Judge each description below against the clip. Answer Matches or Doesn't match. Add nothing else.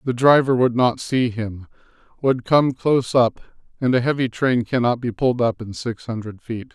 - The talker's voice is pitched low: Matches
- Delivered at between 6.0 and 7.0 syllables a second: Doesn't match